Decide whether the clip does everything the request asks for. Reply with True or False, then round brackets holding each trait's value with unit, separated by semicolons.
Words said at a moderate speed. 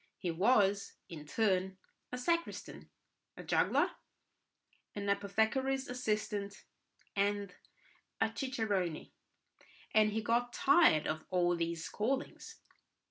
False (100 wpm)